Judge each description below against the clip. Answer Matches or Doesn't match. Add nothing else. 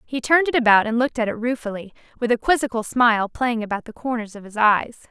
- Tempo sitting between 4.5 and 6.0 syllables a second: Doesn't match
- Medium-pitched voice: Doesn't match